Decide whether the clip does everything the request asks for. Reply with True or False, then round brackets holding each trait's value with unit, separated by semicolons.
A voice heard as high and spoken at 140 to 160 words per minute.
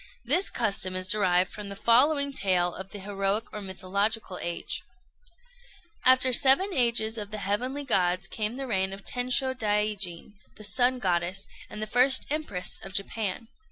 True (210 Hz; 155 wpm)